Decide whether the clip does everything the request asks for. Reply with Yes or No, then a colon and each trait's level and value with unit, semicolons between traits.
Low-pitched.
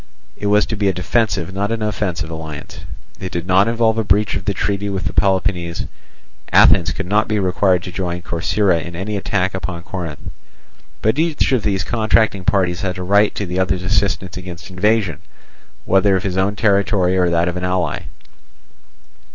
Yes: very low, 95 Hz